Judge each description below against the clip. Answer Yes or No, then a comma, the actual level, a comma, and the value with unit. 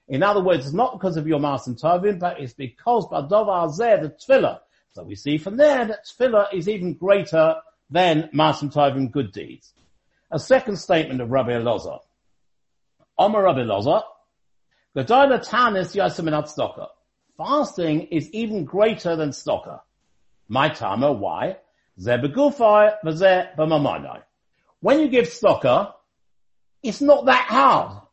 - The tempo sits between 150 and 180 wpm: No, slow, 135 wpm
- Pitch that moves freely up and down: Yes, wide, 7.0 semitones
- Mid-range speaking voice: Yes, medium, 175 Hz